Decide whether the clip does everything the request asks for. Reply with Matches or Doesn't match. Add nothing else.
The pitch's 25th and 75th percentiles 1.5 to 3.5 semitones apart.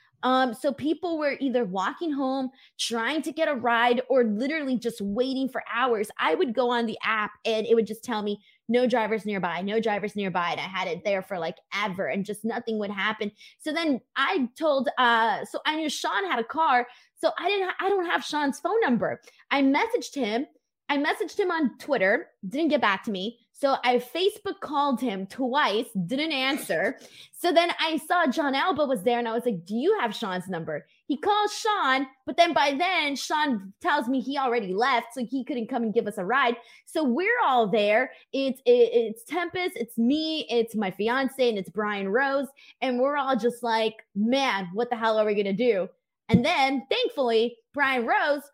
Doesn't match